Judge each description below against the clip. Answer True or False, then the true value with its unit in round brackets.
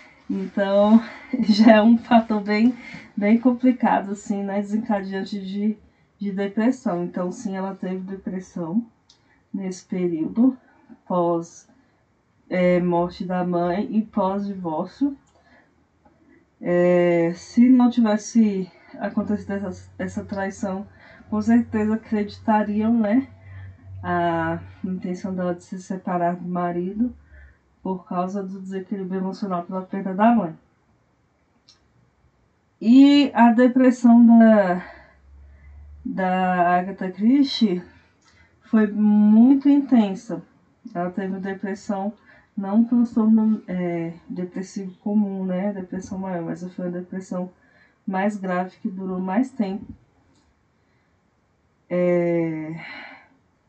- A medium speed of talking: False (105 wpm)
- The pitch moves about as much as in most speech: True (3.5 semitones)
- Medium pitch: False (195 Hz)